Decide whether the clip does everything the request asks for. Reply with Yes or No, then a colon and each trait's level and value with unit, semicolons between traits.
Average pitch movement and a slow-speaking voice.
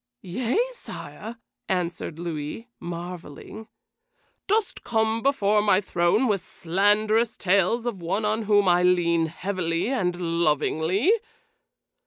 Yes: average, 4.3 semitones; slow, 110 wpm